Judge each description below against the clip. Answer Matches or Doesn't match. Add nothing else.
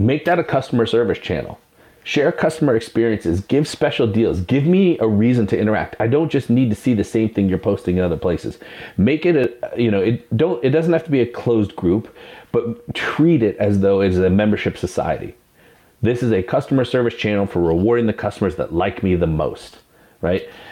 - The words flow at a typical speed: Doesn't match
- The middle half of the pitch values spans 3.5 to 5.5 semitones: Matches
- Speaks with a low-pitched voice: Matches